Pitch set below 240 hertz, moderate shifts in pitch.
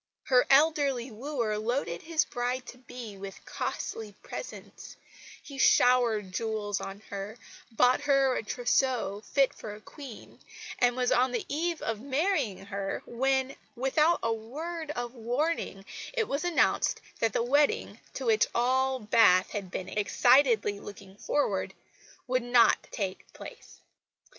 No: high, 245 Hz; average, 4.3 semitones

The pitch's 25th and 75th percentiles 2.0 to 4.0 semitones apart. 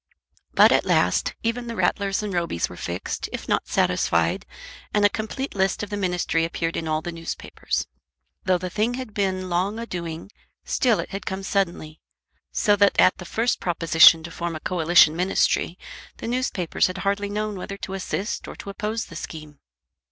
Yes: average, 3.6 semitones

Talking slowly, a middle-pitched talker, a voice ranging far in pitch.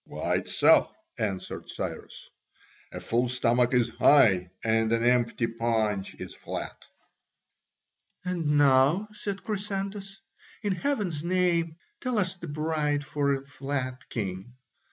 Yes: slow, 120 wpm; medium, 145 Hz; wide, 7.4 semitones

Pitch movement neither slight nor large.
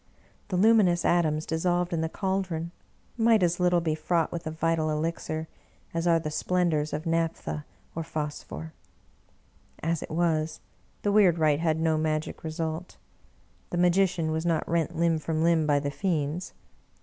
No: narrow, 1.9 semitones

